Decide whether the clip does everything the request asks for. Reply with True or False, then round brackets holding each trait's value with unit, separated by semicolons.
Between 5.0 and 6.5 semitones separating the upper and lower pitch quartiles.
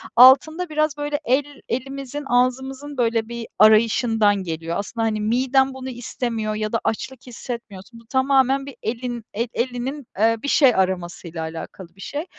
False (3.6 semitones)